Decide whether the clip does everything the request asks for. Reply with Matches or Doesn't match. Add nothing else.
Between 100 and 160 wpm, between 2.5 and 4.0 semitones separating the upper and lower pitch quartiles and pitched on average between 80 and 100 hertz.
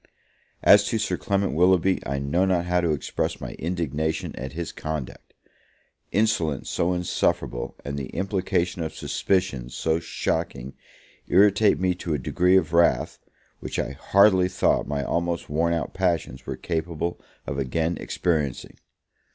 Matches